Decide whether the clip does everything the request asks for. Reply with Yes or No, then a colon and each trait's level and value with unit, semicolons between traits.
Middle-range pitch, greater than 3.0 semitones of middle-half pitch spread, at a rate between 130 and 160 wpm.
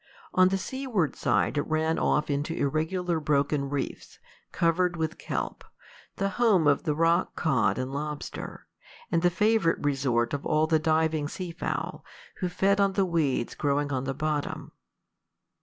Yes: medium, 160 Hz; average, 3.7 semitones; average, 155 wpm